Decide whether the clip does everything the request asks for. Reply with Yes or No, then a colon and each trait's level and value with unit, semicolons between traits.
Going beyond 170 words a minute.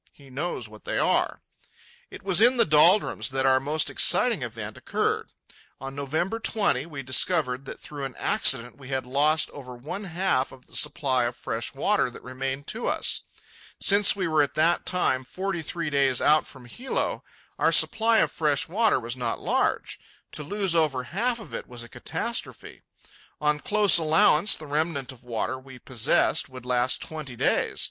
Yes: average, 180 wpm